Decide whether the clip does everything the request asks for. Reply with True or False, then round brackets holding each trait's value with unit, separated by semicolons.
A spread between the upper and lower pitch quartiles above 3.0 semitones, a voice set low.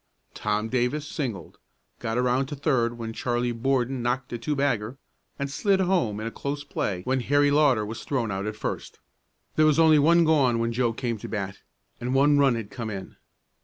True (3.9 semitones; 125 Hz)